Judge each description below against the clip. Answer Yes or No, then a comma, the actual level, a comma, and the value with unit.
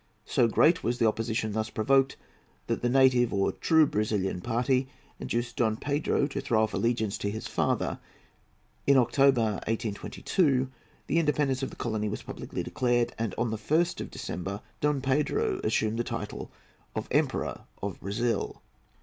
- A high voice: No, low, 120 Hz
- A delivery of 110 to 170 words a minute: Yes, average, 160 wpm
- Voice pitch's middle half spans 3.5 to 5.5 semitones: Yes, average, 3.8 semitones